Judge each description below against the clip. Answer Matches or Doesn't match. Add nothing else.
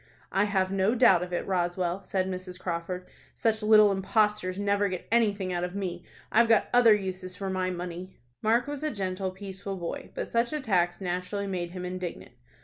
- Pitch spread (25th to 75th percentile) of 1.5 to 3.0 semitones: Matches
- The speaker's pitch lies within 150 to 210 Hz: Matches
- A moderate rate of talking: Matches